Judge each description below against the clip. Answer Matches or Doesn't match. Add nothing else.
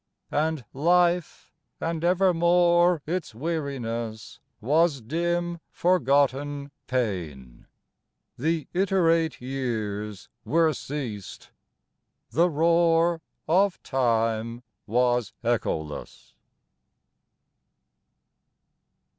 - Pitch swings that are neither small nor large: Doesn't match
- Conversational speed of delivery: Doesn't match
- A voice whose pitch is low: Doesn't match